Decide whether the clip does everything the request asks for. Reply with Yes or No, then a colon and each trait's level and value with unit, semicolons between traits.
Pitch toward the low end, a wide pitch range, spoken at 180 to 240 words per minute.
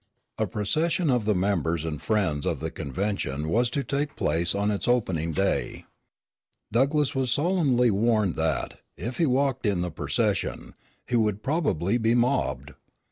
No: low, 105 Hz; wide, 7.2 semitones; average, 155 wpm